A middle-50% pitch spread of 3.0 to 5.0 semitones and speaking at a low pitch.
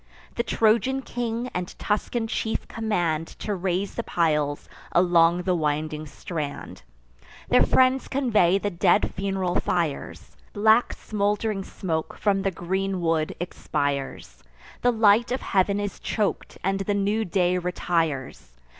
No: average, 4.2 semitones; high, 190 Hz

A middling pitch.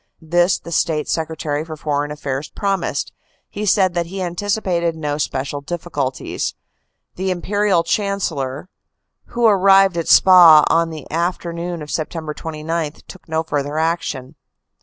Yes: medium, 165 Hz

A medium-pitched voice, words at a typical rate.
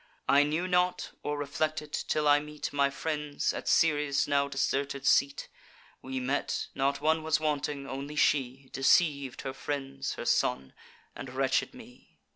Yes: medium, 145 Hz; average, 150 wpm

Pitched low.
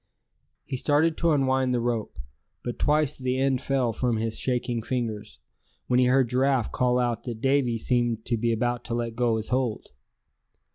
Yes: low, 125 Hz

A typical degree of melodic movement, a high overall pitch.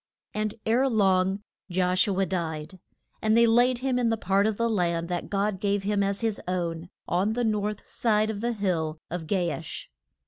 Yes: average, 3.4 semitones; high, 200 Hz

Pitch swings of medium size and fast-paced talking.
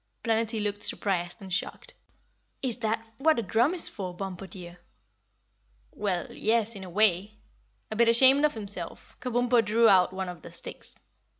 No: average, 3.5 semitones; average, 170 wpm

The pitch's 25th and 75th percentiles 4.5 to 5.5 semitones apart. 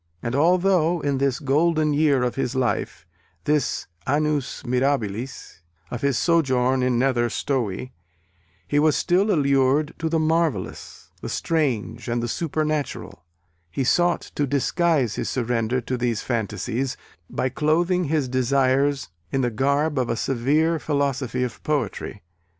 No: average, 3.6 semitones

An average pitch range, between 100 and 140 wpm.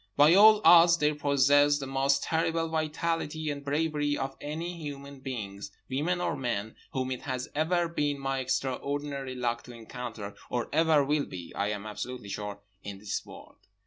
No: average, 3.7 semitones; average, 170 wpm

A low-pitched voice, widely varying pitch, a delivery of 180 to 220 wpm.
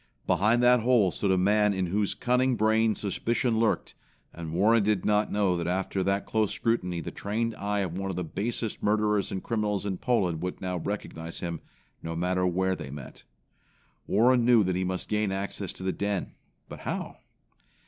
No: low, 100 Hz; average, 3.1 semitones; average, 190 wpm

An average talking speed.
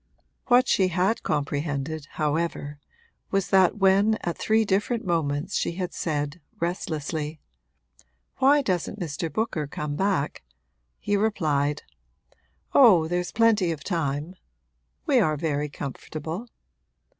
No: slow, 115 wpm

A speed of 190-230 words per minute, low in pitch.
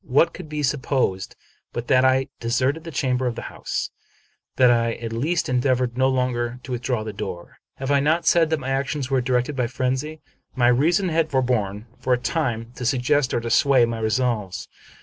Yes: average, 200 wpm; low, 130 Hz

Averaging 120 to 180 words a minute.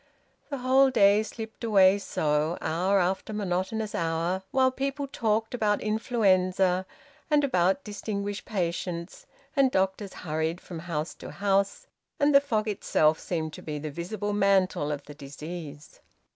Yes: average, 145 wpm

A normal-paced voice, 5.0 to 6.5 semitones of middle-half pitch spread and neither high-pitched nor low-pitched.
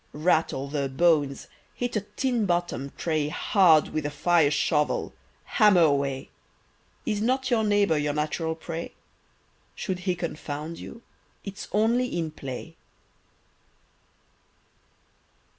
No: slow, 110 wpm; wide, 5.4 semitones; medium, 165 Hz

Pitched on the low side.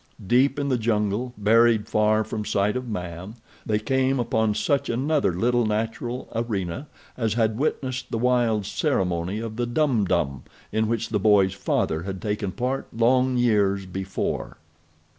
Yes: low, 110 Hz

